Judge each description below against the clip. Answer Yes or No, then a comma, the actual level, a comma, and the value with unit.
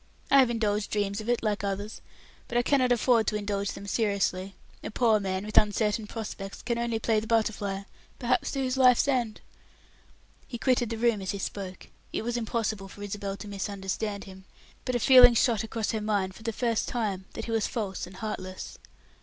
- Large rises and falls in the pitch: No, average, 2.9 semitones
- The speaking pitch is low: No, high, 215 Hz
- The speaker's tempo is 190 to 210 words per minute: Yes, average, 200 wpm